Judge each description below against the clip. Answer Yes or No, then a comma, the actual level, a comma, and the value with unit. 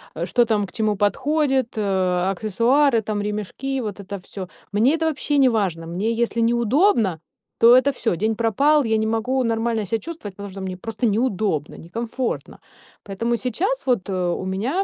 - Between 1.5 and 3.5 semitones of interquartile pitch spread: No, average, 4.2 semitones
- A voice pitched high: Yes, high, 225 Hz